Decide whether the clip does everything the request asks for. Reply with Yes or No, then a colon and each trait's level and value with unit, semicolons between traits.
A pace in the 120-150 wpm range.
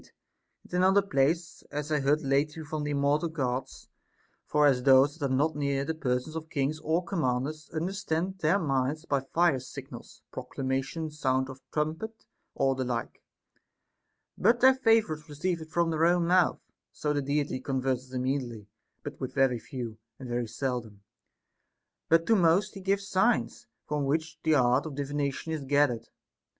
No: average, 165 wpm